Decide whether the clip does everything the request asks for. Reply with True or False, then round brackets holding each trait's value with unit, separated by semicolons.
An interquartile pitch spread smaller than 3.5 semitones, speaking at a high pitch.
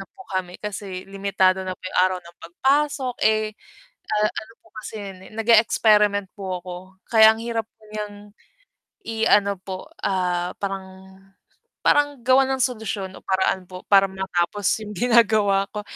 True (2.7 semitones; 205 Hz)